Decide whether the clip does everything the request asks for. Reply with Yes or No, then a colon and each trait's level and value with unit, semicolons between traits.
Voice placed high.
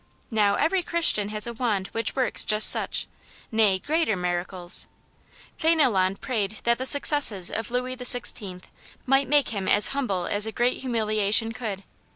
Yes: high, 220 Hz